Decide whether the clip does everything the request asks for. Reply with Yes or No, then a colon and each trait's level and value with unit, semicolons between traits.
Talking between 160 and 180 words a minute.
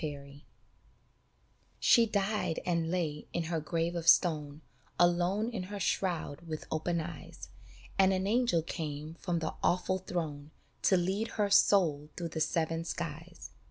No: average, 145 wpm